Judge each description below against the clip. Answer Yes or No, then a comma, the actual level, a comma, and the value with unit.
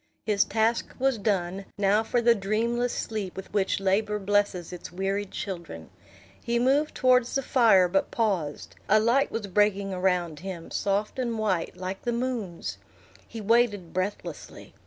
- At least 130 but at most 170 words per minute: Yes, average, 155 wpm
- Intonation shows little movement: No, average, 3.5 semitones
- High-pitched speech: Yes, high, 205 Hz